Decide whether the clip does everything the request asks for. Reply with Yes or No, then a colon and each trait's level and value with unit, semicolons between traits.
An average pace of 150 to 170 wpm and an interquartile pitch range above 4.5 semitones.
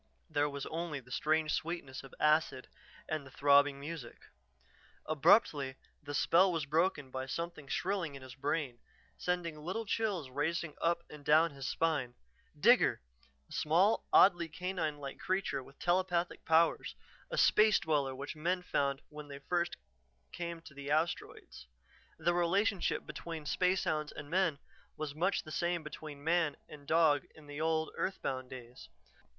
No: average, 155 wpm; average, 3.3 semitones